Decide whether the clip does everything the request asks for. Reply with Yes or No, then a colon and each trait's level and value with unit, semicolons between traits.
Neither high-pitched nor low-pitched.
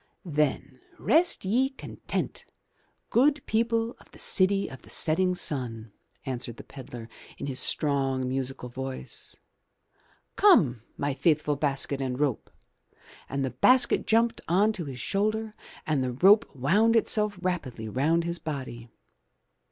Yes: medium, 150 Hz